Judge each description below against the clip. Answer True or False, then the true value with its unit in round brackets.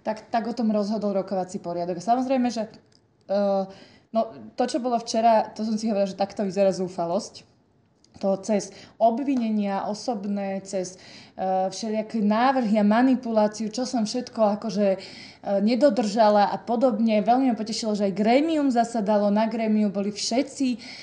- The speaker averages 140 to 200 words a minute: True (150 wpm)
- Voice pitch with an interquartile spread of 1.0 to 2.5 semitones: False (2.9 semitones)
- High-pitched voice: True (215 Hz)